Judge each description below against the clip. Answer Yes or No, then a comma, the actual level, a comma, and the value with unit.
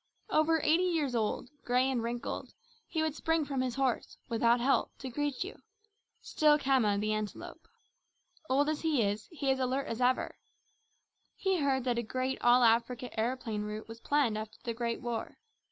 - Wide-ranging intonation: No, average, 3.7 semitones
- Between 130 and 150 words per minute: No, average, 180 wpm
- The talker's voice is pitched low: No, very high, 255 Hz